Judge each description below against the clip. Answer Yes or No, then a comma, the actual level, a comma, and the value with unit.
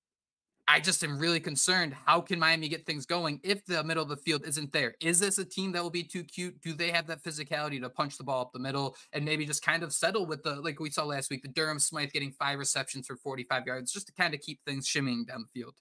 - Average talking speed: No, fast, 275 wpm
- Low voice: No, medium, 155 Hz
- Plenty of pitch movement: No, average, 3.3 semitones